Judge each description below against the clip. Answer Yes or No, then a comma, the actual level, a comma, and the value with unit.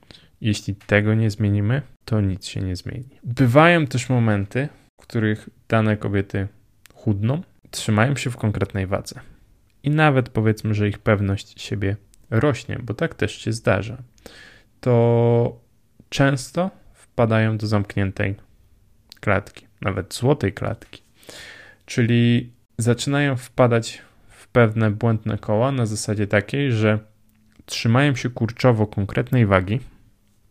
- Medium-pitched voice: No, low, 110 Hz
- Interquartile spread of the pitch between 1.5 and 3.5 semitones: Yes, average, 3.2 semitones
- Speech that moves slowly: No, average, 120 wpm